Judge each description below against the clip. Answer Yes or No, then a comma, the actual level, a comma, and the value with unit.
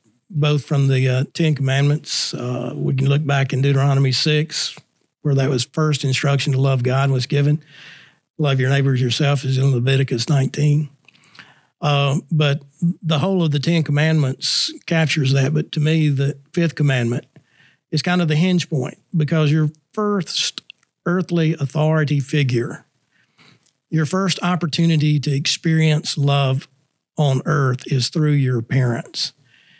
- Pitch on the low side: No, medium, 145 Hz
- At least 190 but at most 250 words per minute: No, average, 145 wpm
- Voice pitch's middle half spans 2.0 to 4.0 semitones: Yes, narrow, 2.6 semitones